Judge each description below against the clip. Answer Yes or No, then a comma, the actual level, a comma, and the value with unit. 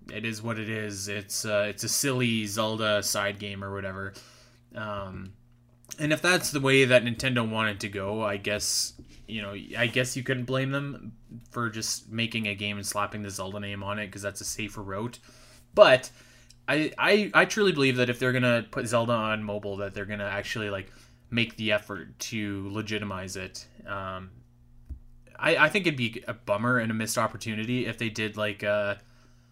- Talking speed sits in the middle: Yes, average, 195 wpm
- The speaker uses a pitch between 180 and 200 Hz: No, low, 110 Hz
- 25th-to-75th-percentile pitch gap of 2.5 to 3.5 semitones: Yes, average, 3.2 semitones